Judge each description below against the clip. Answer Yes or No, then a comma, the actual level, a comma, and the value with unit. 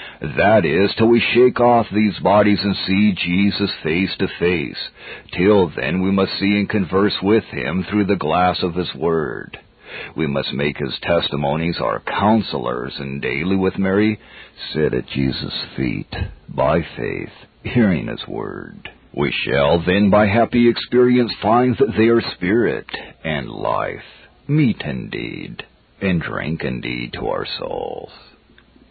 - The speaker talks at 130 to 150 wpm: Yes, average, 145 wpm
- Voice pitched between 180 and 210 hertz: No, low, 100 Hz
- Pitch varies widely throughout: No, average, 3.7 semitones